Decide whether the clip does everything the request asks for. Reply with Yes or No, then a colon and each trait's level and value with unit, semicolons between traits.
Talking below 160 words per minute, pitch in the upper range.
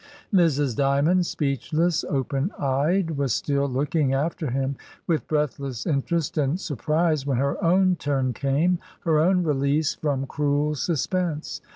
No: average, 140 wpm; medium, 150 Hz